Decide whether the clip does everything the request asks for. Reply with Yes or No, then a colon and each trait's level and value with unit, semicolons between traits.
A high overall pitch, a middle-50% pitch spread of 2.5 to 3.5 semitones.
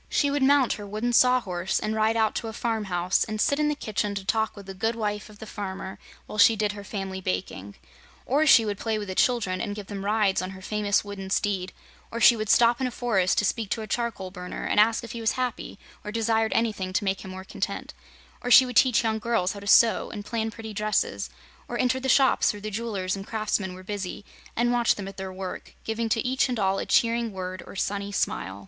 Yes: high, 215 Hz; average, 3.2 semitones